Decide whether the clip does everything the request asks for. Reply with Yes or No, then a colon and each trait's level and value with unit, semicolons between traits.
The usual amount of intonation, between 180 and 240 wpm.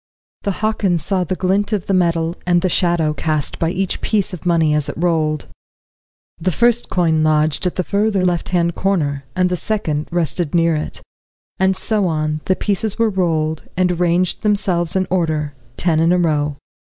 Yes: average, 3.1 semitones; average, 185 wpm